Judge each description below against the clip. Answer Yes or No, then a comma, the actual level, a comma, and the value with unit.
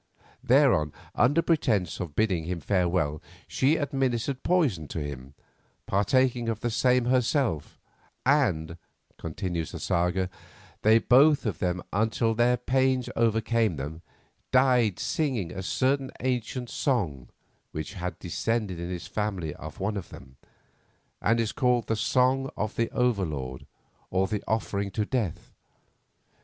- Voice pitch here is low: Yes, low, 110 Hz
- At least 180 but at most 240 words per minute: No, slow, 135 wpm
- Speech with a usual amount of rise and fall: No, wide, 6.2 semitones